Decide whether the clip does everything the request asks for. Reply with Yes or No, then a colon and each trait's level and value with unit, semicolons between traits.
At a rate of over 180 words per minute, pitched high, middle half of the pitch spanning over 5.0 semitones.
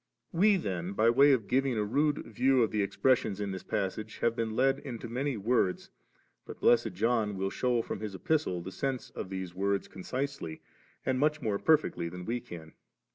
No: average, 190 wpm; low, 115 Hz; wide, 5.4 semitones